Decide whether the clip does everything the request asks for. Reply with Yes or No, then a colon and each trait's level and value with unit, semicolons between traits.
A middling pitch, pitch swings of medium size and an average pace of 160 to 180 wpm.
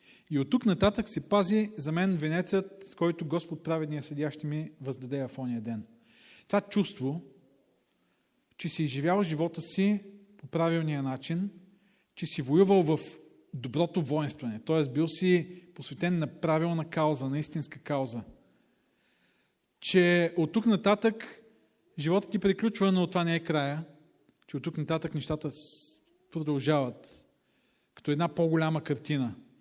No: medium, 165 Hz; average, 4.0 semitones; average, 135 wpm